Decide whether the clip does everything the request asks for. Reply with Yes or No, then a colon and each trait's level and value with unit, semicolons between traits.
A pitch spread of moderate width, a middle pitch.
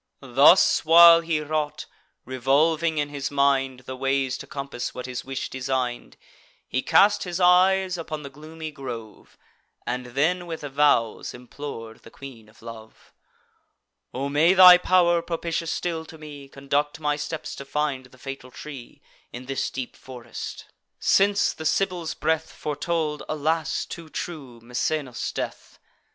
Yes: average, 3.9 semitones; medium, 145 Hz